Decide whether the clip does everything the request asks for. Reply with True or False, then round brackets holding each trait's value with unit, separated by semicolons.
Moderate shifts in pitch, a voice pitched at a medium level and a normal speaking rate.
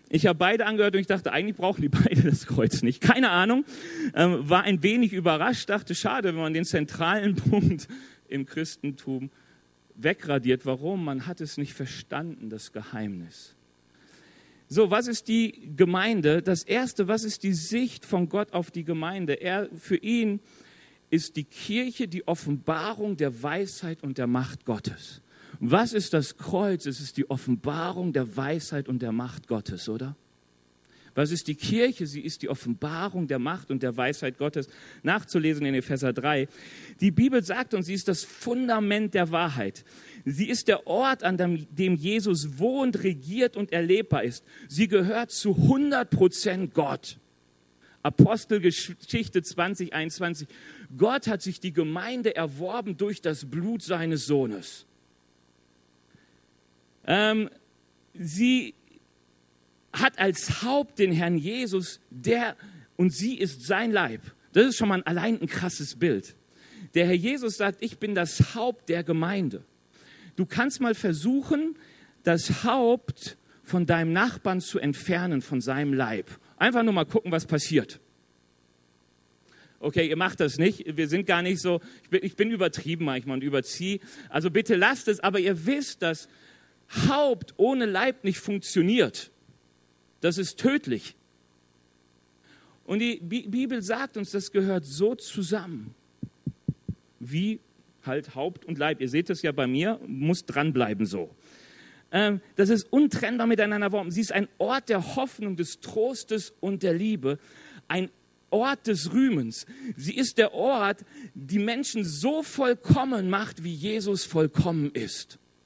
False (6.8 semitones; 175 Hz; 150 wpm)